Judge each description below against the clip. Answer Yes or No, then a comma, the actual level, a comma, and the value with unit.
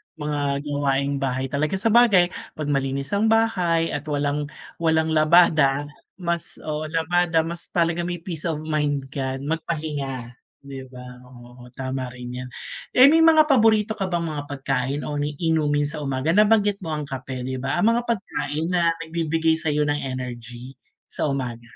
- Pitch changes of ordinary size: Yes, average, 3.9 semitones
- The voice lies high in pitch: No, medium, 150 Hz